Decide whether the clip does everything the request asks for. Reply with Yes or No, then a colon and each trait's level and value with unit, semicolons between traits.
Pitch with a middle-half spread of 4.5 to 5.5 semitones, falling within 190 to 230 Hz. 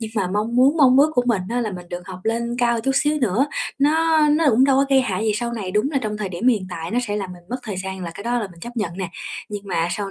Yes: average, 5.0 semitones; high, 220 Hz